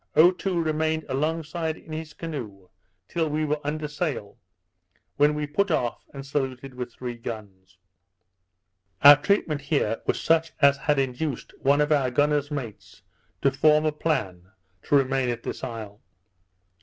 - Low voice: No, medium, 145 Hz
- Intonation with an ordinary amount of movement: Yes, average, 3.7 semitones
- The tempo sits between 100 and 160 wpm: Yes, average, 155 wpm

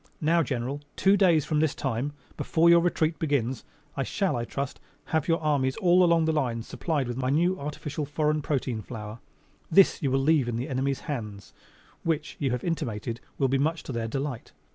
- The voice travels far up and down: No, average, 4.1 semitones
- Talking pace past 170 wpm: Yes, average, 195 wpm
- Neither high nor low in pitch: Yes, medium, 145 Hz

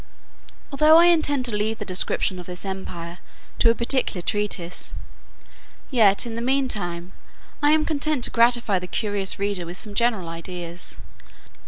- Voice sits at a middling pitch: No, high, 210 Hz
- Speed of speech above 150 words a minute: Yes, average, 160 wpm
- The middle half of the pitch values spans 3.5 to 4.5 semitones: No, wide, 5.6 semitones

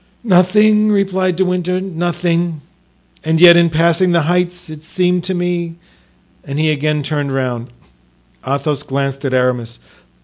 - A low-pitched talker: No, medium, 170 Hz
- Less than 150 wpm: Yes, average, 140 wpm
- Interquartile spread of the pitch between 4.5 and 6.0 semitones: No, average, 3.7 semitones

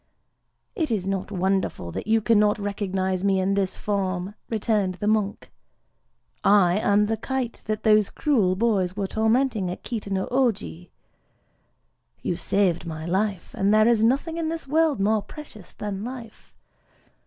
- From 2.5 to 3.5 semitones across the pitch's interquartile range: Yes, average, 2.9 semitones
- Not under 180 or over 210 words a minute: No, average, 155 wpm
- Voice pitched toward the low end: No, high, 205 Hz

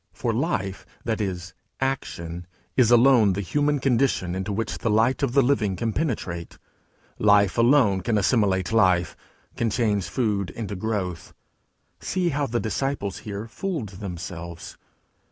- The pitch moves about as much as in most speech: Yes, average, 4.6 semitones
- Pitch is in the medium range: No, low, 105 Hz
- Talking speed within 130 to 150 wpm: Yes, average, 140 wpm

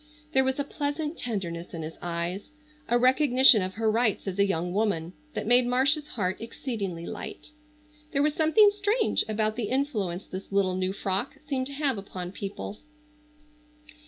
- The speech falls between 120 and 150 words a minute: No, average, 165 wpm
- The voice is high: Yes, high, 220 Hz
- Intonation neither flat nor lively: No, wide, 6.6 semitones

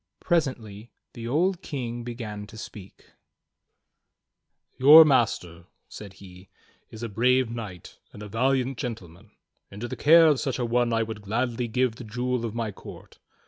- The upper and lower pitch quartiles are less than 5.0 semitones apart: Yes, average, 3.3 semitones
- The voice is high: No, low, 115 Hz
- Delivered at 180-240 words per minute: No, average, 160 wpm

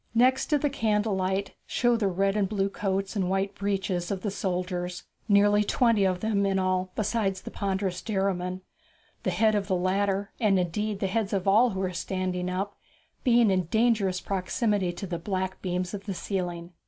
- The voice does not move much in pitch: Yes, narrow, 2.0 semitones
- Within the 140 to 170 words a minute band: No, average, 190 wpm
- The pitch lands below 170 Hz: No, high, 195 Hz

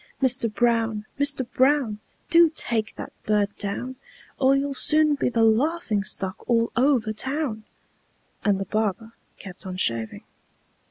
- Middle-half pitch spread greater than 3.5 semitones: Yes, average, 4.5 semitones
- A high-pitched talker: Yes, high, 230 Hz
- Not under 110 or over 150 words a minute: Yes, average, 140 wpm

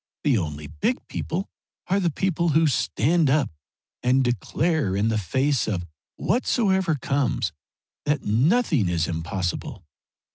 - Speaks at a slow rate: Yes, slow, 130 wpm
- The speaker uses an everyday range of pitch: No, wide, 8.9 semitones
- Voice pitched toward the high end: No, low, 135 Hz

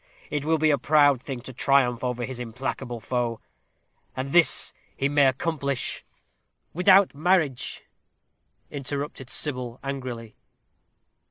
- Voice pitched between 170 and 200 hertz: No, low, 135 Hz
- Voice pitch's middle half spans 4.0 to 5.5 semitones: No, average, 3.0 semitones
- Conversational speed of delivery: No, slow, 120 wpm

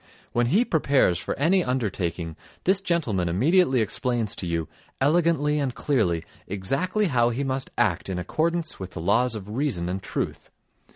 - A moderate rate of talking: Yes, average, 160 wpm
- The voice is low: Yes, low, 125 Hz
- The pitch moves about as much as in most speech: No, wide, 8.1 semitones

